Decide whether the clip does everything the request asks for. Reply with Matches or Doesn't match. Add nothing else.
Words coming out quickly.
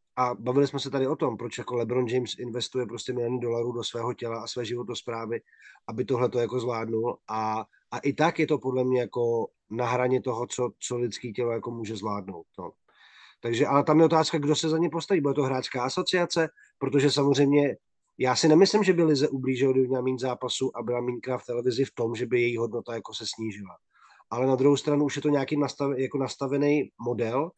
Matches